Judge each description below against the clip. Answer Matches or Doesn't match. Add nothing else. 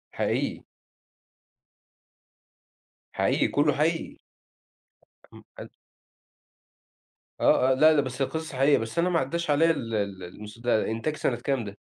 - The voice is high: Doesn't match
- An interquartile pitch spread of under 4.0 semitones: Doesn't match